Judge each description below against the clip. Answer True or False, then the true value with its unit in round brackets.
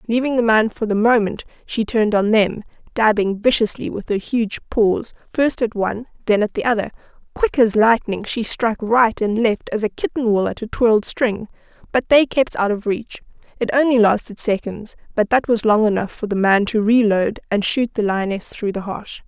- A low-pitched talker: False (220 Hz)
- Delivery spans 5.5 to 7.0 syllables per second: False (5.0 syllables/s)